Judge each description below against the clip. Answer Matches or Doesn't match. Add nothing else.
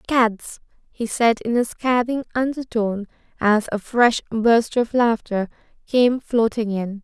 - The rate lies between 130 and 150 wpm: Matches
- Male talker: Doesn't match